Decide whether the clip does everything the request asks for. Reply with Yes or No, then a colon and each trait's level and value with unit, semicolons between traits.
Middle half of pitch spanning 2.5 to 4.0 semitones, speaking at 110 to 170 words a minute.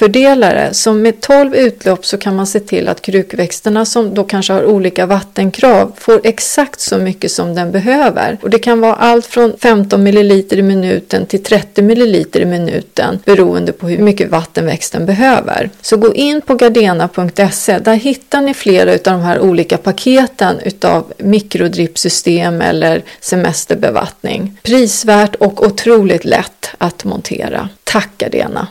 Yes: average, 3.6 semitones; average, 155 wpm